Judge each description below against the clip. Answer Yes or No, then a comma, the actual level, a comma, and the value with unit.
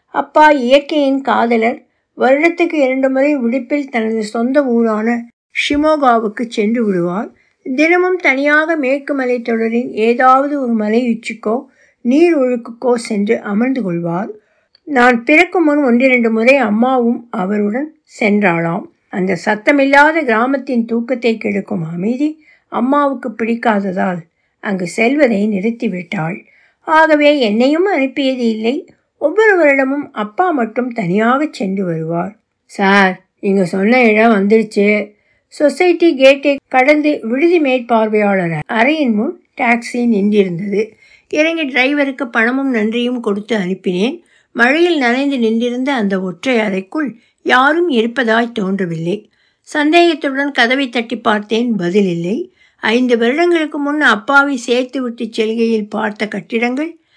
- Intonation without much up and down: No, average, 4.6 semitones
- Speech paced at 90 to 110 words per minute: Yes, average, 105 wpm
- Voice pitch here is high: Yes, high, 240 Hz